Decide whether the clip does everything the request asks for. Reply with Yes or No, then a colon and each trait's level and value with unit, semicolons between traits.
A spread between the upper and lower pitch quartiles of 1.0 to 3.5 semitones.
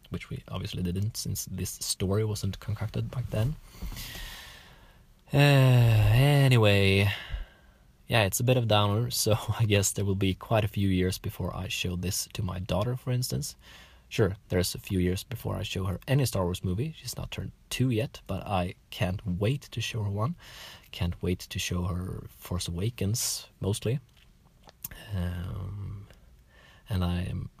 No: average, 4.1 semitones